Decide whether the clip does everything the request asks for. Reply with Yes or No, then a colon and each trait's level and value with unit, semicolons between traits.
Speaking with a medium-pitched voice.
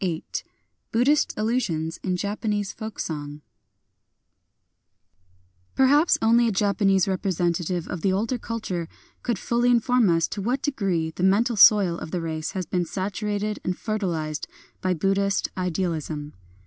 No: high, 195 Hz